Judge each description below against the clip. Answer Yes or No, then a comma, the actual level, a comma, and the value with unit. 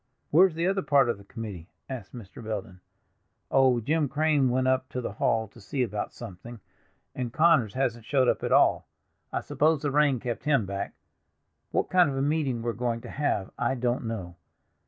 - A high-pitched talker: No, low, 125 Hz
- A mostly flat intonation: No, average, 4.2 semitones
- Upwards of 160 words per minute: Yes, average, 200 wpm